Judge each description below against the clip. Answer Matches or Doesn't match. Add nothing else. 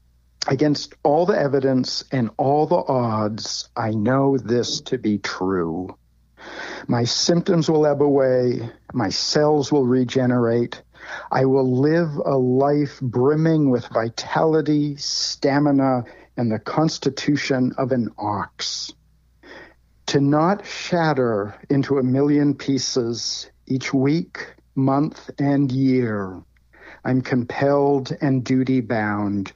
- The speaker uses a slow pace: Matches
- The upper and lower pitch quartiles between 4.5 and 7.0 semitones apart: Doesn't match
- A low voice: Matches